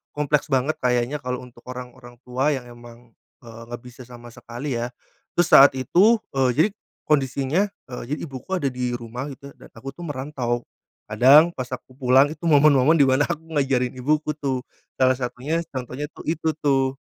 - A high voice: No, low, 130 Hz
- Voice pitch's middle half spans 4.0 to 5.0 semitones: No, average, 2.9 semitones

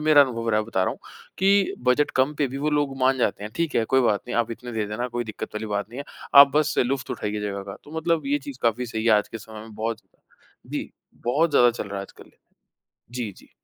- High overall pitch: No, low, 120 Hz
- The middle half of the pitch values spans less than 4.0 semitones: No, average, 4.5 semitones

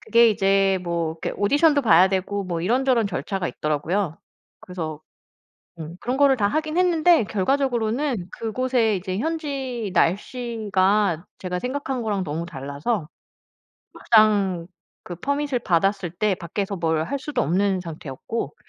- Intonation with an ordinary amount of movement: No, wide, 5.9 semitones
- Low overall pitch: No, high, 200 Hz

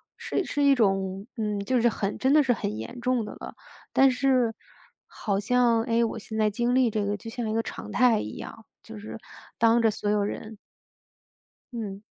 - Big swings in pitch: No, average, 3.2 semitones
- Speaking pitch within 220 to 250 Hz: Yes, high, 225 Hz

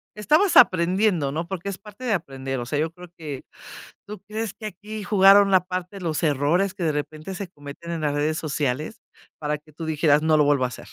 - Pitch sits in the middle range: Yes, medium, 170 Hz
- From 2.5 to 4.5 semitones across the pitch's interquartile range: No, average, 4.9 semitones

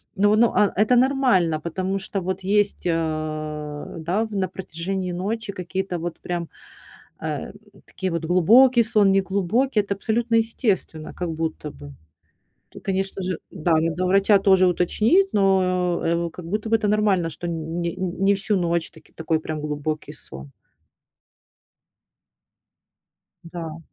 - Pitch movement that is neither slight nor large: Yes, average, 3.7 semitones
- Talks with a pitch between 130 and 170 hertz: No, medium, 185 Hz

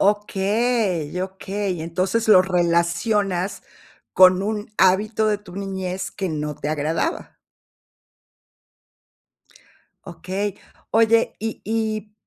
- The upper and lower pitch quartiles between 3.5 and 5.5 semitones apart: No, average, 2.9 semitones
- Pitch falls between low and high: No, high, 195 Hz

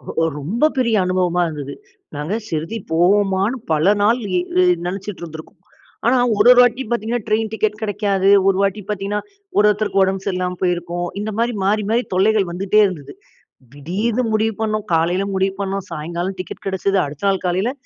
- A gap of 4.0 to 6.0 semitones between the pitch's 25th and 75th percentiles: No, average, 3.2 semitones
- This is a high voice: Yes, high, 195 Hz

